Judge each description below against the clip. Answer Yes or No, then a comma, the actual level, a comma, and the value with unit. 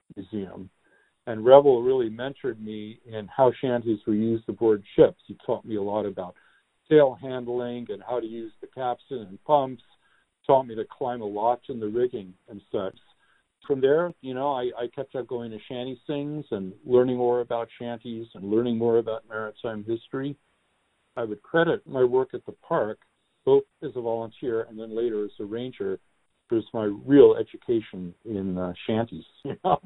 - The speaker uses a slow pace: No, average, 180 wpm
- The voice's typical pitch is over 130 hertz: No, low, 120 Hz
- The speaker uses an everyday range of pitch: Yes, average, 3.8 semitones